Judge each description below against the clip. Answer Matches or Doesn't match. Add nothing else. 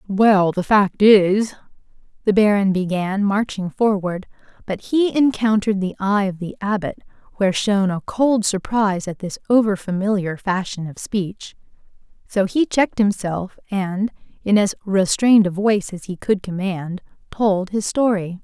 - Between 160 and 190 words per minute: Doesn't match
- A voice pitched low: Doesn't match